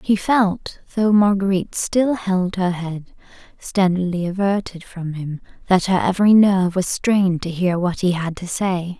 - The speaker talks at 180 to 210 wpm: No, average, 165 wpm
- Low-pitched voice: No, medium, 185 Hz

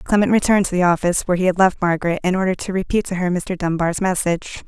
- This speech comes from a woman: Yes, female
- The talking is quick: Yes, fast, 245 wpm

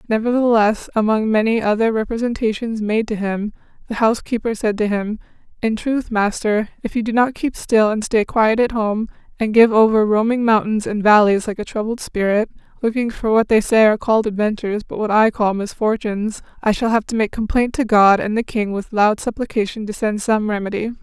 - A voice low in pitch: No, high, 220 Hz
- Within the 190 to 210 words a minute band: Yes, average, 195 wpm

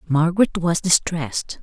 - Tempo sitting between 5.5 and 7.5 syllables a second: No, 4.8 syllables/s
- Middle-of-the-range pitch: Yes, medium, 165 Hz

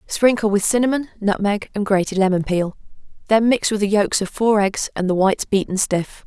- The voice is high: Yes, high, 205 Hz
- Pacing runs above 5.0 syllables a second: Yes, 5.4 syllables/s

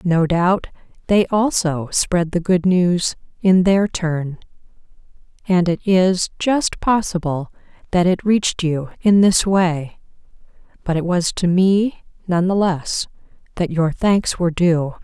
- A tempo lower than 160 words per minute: Yes, average, 145 wpm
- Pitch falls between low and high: Yes, medium, 180 Hz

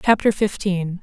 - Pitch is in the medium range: No, high, 195 Hz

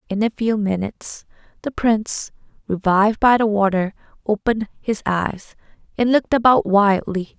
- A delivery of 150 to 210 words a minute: No, average, 140 wpm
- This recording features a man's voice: No, female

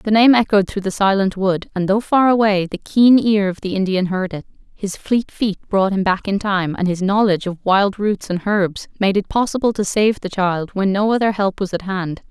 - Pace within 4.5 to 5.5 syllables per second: Yes, 5.0 syllables/s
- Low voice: No, high, 200 Hz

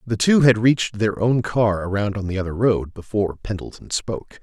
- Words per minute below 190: No, fast, 205 wpm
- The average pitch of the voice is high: No, low, 110 Hz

